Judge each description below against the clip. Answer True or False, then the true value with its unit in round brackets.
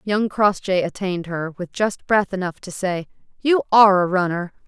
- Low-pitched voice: False (190 Hz)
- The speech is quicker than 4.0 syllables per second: True (4.9 syllables/s)